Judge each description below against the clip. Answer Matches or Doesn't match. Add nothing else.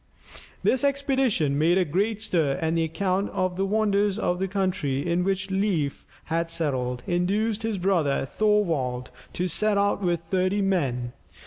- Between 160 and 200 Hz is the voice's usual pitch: Matches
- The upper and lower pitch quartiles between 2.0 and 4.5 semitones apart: Matches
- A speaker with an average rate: Matches